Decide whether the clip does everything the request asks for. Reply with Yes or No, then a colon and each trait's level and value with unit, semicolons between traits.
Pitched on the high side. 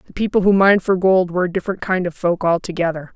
No: medium, 180 Hz